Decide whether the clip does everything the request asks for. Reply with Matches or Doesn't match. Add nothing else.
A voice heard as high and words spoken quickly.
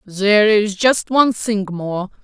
Doesn't match